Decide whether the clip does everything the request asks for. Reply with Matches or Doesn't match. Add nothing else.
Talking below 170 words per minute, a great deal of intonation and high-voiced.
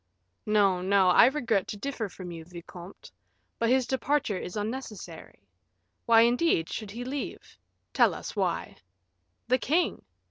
Matches